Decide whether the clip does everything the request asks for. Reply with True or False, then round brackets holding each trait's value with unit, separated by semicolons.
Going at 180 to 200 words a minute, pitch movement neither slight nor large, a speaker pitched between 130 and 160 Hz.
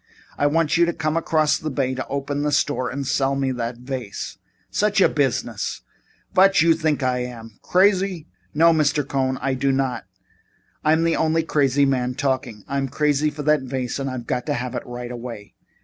True (195 wpm; 3.5 semitones; 140 Hz)